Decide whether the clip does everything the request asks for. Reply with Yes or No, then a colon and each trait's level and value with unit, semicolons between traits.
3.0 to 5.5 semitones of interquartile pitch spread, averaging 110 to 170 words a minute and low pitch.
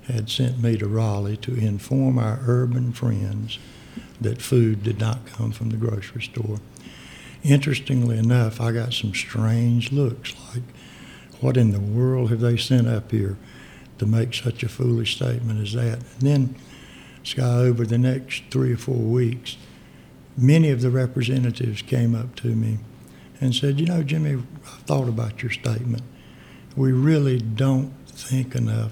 No: narrow, 2.4 semitones; average, 160 wpm; low, 120 Hz